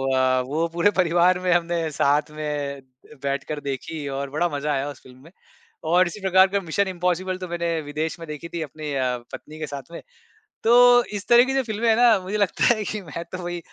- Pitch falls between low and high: Yes, medium, 170 Hz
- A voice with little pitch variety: No, average, 4.0 semitones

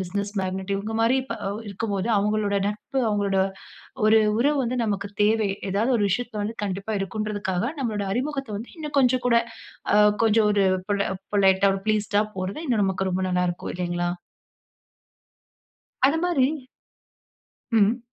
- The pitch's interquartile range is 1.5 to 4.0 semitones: Yes, average, 2.9 semitones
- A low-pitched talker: No, high, 210 Hz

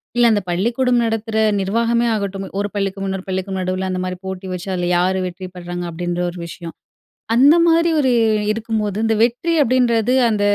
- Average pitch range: Yes, average, 4.1 semitones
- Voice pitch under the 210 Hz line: Yes, high, 200 Hz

